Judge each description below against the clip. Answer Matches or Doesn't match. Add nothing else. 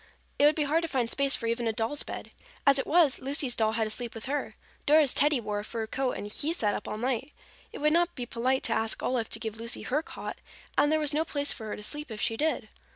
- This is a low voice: Doesn't match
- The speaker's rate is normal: Doesn't match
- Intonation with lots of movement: Doesn't match